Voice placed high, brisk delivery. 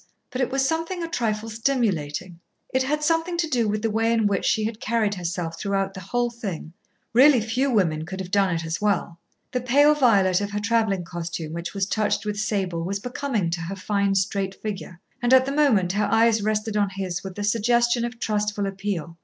Yes: high, 210 Hz; fast, 210 wpm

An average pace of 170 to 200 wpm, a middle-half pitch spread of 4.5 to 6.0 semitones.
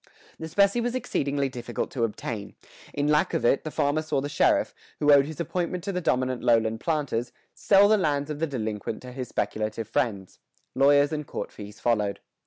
Yes: average, 195 wpm; average, 5.0 semitones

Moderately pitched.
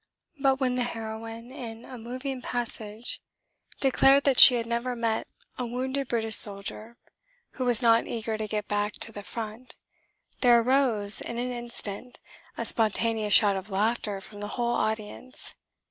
No: high, 230 Hz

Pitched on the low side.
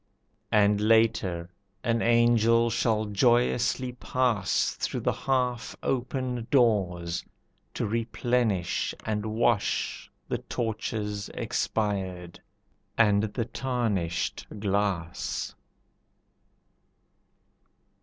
Yes: low, 110 Hz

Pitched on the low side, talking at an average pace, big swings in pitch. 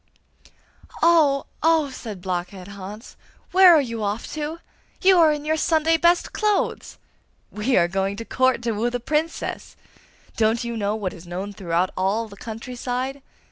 No: high, 235 Hz; average, 165 wpm; wide, 7.1 semitones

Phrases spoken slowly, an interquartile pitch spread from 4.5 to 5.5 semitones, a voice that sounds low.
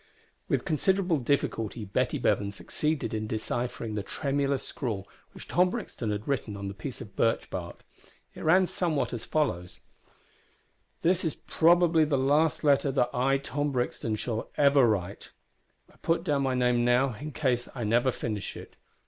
No: average, 165 wpm; average, 5.2 semitones; low, 130 Hz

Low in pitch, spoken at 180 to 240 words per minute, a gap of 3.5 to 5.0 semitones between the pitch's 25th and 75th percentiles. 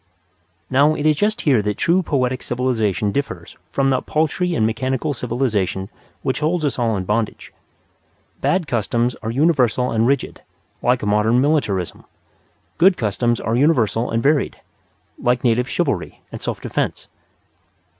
No: low, 125 Hz; average, 145 wpm; average, 4.5 semitones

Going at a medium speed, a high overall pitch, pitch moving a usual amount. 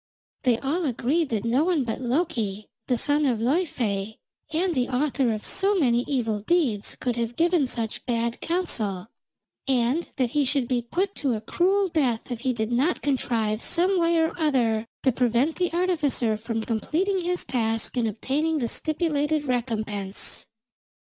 No: average, 165 wpm; very high, 255 Hz; wide, 5.9 semitones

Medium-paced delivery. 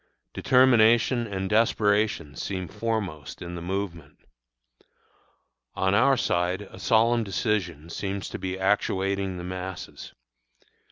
No: slow, 110 wpm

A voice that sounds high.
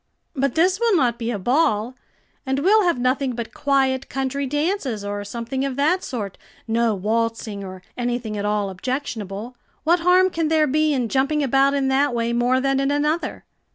Yes: very high, 260 Hz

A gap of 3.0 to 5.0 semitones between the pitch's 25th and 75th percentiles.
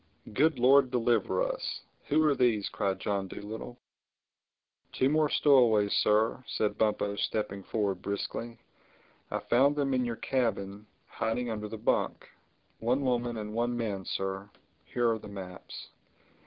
Yes: average, 3.7 semitones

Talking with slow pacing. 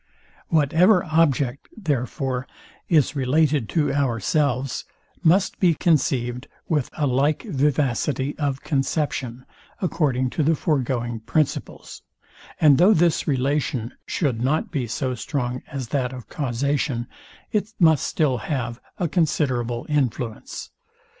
Yes: slow, 115 wpm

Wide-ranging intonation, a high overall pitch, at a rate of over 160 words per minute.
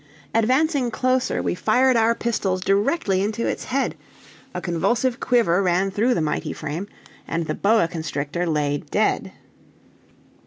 No: wide, 6.1 semitones; high, 205 Hz; average, 140 wpm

